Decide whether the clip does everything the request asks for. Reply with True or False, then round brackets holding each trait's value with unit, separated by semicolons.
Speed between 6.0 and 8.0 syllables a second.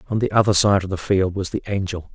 True (6.3 syllables/s)